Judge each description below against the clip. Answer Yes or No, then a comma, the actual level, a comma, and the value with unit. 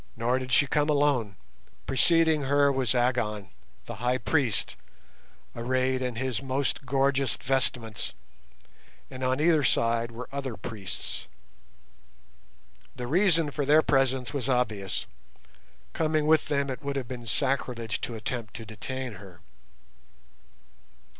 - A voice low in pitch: Yes, low, 130 Hz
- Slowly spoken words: Yes, slow, 125 wpm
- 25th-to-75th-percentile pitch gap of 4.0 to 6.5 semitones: No, average, 3.4 semitones